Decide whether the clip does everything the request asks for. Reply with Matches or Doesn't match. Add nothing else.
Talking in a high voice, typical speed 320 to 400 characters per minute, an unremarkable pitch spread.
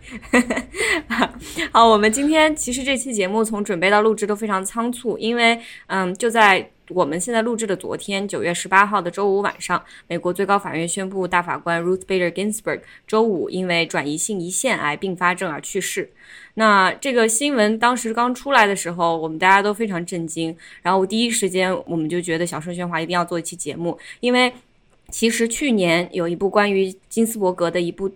Matches